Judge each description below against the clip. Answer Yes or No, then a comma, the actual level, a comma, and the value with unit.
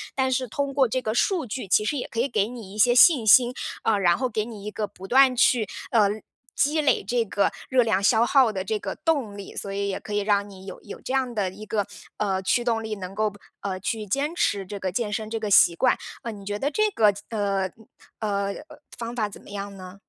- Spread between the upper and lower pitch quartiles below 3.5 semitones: No, average, 3.8 semitones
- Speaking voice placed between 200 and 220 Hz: Yes, high, 215 Hz